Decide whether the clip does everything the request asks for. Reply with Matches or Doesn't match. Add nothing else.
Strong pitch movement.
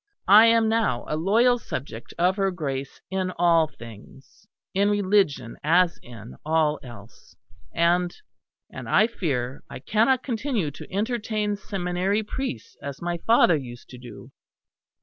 Matches